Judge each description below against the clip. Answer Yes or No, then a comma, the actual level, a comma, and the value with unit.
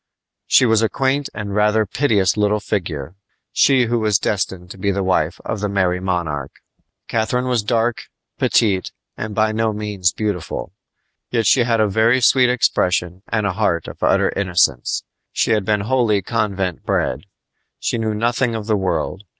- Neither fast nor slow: Yes, average, 170 wpm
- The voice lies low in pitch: Yes, low, 105 Hz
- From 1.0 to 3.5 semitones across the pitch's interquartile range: Yes, average, 3.2 semitones